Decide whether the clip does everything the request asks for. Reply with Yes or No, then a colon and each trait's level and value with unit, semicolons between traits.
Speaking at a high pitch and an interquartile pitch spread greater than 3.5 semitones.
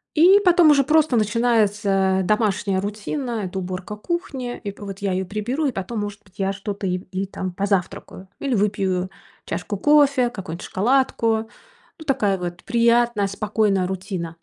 Yes: high, 205 Hz; average, 4.0 semitones